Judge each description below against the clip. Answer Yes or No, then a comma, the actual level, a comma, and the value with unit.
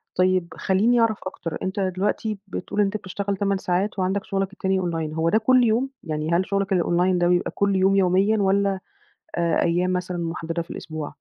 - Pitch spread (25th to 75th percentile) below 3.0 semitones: Yes, narrow, 2.4 semitones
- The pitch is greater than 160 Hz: Yes, high, 190 Hz